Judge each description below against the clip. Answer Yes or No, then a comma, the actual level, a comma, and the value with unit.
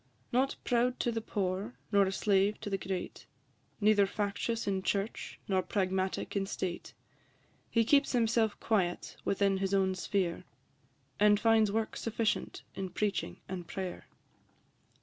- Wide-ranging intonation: No, average, 2.7 semitones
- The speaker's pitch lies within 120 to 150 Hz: No, high, 200 Hz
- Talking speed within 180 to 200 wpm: No, average, 140 wpm